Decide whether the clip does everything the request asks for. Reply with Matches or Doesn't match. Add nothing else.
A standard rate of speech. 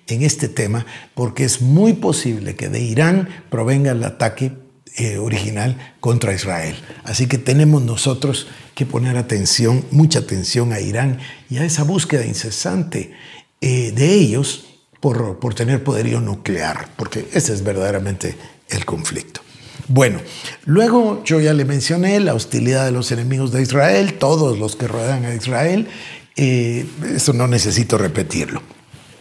Matches